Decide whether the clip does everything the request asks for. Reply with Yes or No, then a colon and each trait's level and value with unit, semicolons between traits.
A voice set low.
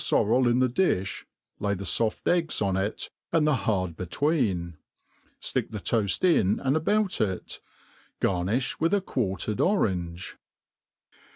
Yes: low, 110 Hz